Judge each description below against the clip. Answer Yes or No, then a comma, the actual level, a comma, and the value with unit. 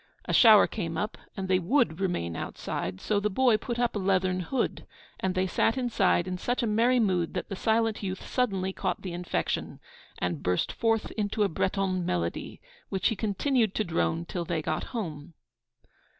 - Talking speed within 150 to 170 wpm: No, average, 185 wpm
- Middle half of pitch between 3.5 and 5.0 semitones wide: Yes, average, 4.2 semitones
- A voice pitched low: No, high, 190 Hz